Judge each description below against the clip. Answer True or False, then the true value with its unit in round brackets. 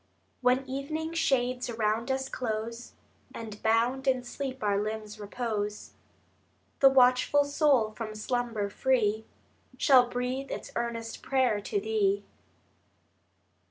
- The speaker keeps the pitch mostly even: False (3.4 semitones)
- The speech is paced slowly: True (125 wpm)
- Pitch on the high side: True (245 Hz)